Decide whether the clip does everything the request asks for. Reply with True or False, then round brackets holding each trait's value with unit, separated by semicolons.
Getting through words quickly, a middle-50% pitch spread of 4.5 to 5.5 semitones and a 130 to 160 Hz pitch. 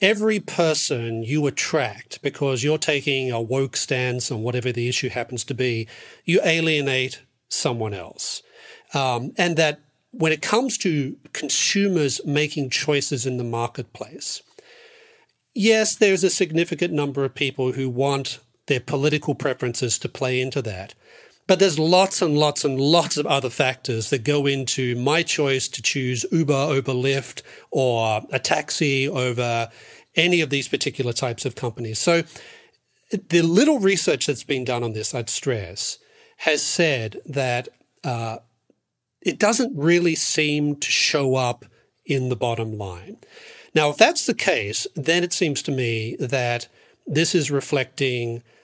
False (150 wpm; 5.0 semitones; 140 Hz)